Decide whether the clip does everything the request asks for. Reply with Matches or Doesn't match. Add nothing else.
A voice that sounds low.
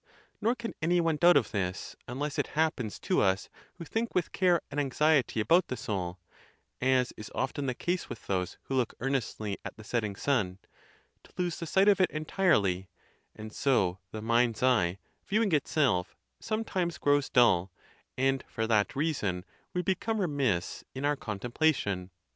Matches